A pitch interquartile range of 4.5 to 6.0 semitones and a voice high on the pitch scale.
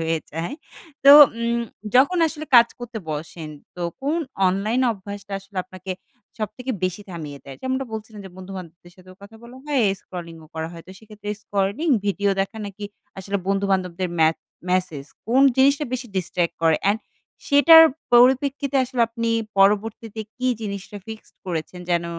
Yes: average, 4.9 semitones; high, 200 Hz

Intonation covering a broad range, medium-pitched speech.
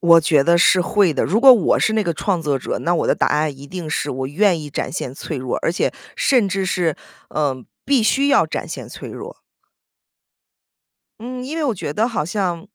Yes: wide, 6.3 semitones; medium, 175 Hz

